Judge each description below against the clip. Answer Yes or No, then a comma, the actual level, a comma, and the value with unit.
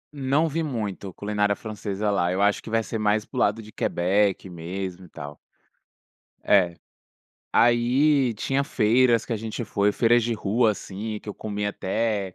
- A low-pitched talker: Yes, low, 105 Hz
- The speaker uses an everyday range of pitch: Yes, average, 3.0 semitones